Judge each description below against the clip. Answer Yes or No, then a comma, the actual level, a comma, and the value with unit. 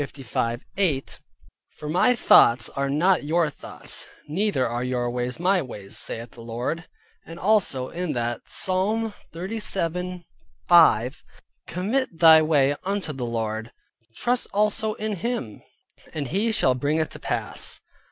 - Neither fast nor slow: No, slow, 130 wpm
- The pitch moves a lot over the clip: Yes, wide, 7.3 semitones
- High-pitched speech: No, medium, 160 Hz